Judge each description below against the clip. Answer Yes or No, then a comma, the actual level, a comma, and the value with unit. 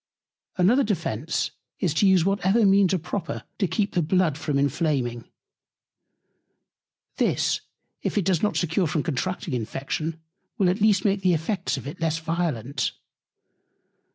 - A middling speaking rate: Yes, average, 145 wpm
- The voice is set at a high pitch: No, medium, 170 Hz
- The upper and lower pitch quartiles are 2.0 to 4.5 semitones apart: Yes, average, 4.1 semitones